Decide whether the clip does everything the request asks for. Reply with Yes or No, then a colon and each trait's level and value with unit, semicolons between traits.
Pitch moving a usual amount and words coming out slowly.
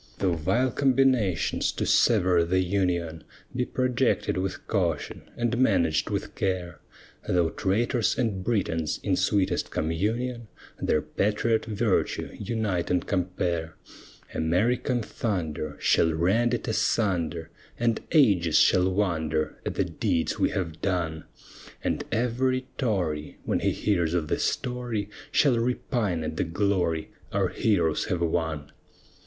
No: wide, 5.7 semitones; slow, 125 wpm